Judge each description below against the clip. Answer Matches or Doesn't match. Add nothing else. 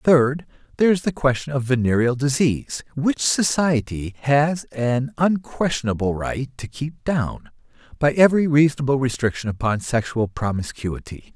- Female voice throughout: Doesn't match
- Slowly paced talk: Matches